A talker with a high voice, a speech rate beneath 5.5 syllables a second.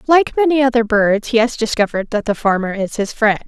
No: high, 230 Hz; 5.9 syllables/s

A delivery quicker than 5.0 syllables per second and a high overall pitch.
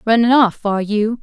Yes: 5.4 syllables/s; high, 220 Hz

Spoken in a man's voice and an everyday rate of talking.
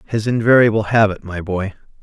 Yes: male; average, 150 wpm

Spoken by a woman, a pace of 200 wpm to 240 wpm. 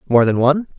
No: male; fast, 230 wpm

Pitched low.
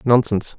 Yes: low, 115 Hz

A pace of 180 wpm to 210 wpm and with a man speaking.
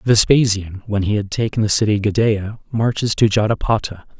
No: average, 155 wpm; male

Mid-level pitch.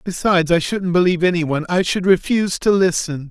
Yes: medium, 175 Hz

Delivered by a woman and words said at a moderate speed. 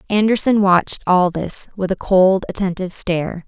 Yes: female; average, 155 wpm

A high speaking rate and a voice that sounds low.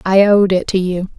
No: fast, 255 wpm; high, 190 Hz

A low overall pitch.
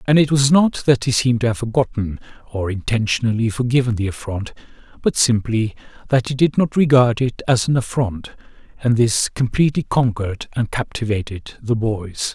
Yes: low, 120 Hz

